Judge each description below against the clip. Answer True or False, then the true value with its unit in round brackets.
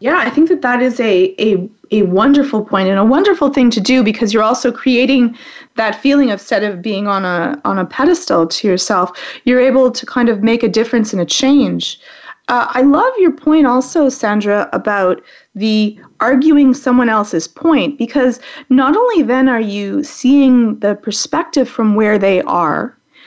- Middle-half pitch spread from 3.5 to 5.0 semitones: True (4.5 semitones)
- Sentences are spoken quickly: False (185 wpm)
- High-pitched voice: True (245 Hz)